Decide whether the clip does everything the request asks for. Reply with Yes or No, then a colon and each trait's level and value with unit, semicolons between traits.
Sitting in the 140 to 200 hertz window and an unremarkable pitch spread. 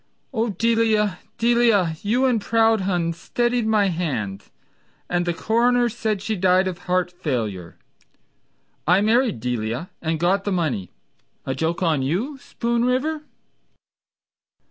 No: high, 190 Hz; wide, 5.7 semitones